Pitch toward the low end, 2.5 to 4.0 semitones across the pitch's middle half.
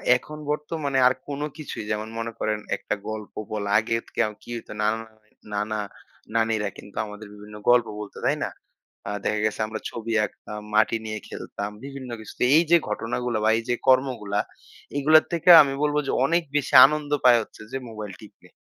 No: low, 115 Hz; average, 4.4 semitones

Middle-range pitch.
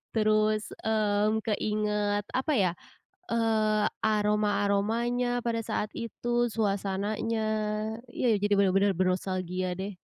No: high, 210 Hz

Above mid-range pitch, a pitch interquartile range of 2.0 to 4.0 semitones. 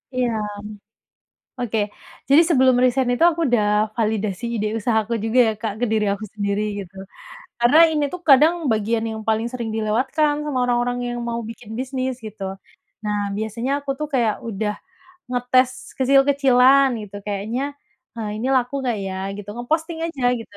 Yes: high, 245 Hz; average, 3.3 semitones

